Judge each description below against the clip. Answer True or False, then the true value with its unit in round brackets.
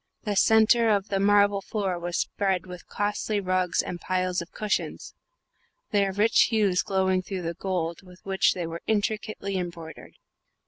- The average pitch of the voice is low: False (190 Hz)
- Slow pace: False (155 wpm)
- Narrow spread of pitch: True (2.3 semitones)